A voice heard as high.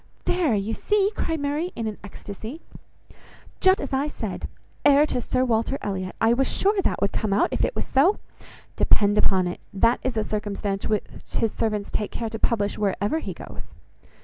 Yes: high, 225 Hz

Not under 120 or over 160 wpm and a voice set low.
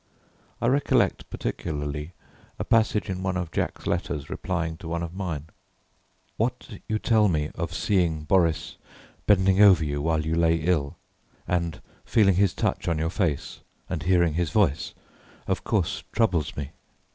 Yes: average, 155 wpm; very low, 85 Hz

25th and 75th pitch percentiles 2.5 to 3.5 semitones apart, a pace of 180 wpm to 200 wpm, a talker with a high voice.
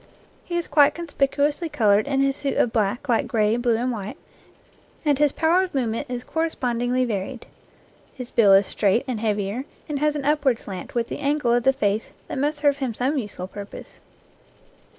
No: average, 4.5 semitones; average, 190 wpm; very high, 250 Hz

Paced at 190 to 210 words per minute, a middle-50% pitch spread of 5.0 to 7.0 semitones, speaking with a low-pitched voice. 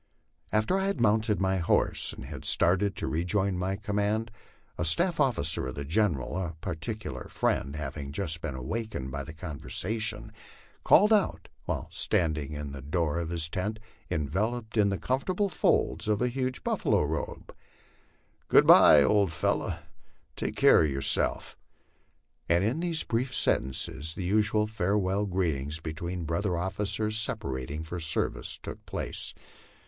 No: average, 150 wpm; wide, 5.6 semitones; very low, 95 Hz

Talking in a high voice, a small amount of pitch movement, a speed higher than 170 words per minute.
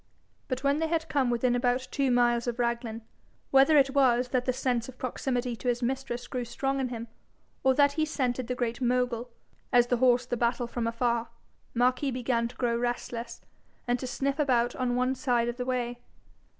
Yes: high, 245 Hz; narrow, 1.7 semitones; average, 200 wpm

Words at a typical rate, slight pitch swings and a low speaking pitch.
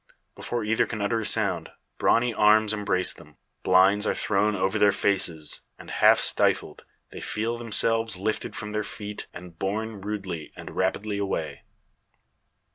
Yes: average, 150 wpm; narrow, 2.2 semitones; low, 105 Hz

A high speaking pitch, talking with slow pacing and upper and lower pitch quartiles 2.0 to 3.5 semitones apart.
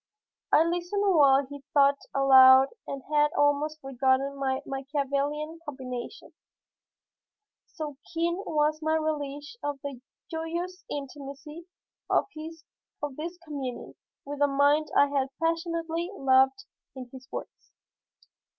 Yes: very high, 290 Hz; slow, 115 wpm; average, 2.9 semitones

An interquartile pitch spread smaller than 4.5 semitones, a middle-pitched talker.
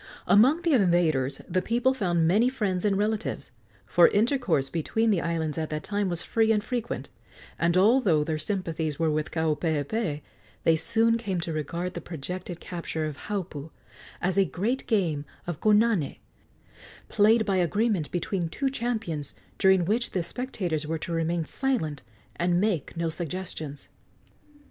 No: average, 5.2 semitones; medium, 180 Hz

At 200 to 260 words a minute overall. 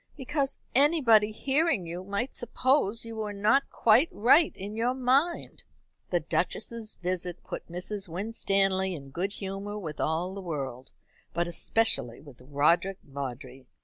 No: average, 140 wpm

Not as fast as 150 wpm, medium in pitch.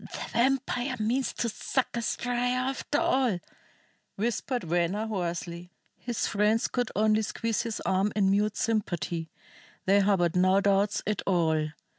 No: average, 140 wpm; high, 210 Hz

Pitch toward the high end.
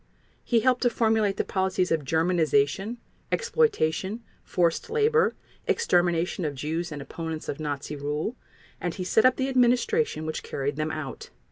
No: medium, 180 Hz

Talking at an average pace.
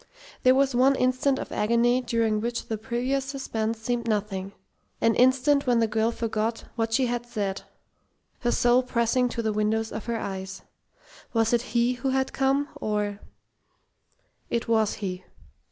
Yes: average, 160 wpm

